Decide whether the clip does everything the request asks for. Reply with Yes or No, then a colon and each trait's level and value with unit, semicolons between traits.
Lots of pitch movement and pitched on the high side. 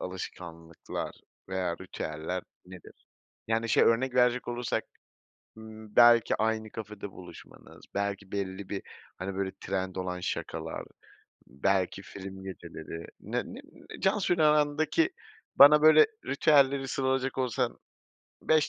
No: wide, 5.9 semitones; low, 105 Hz